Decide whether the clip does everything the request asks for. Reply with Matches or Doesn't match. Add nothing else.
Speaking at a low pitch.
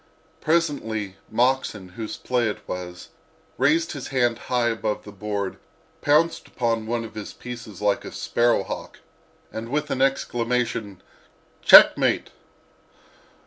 Matches